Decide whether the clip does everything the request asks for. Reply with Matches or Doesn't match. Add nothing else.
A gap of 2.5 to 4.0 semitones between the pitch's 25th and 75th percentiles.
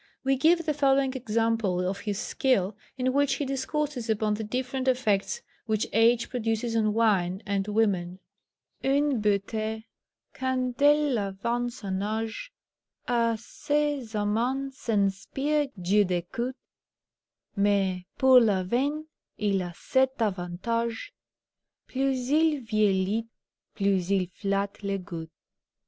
Doesn't match